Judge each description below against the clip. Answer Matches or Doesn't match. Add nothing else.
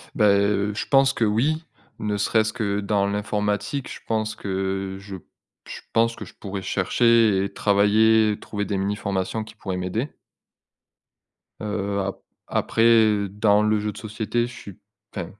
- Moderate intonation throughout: Doesn't match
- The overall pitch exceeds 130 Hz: Doesn't match